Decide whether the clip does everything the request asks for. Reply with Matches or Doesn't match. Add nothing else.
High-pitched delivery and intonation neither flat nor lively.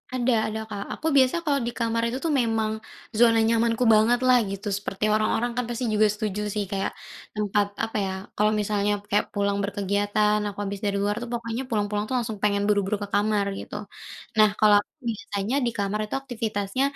Doesn't match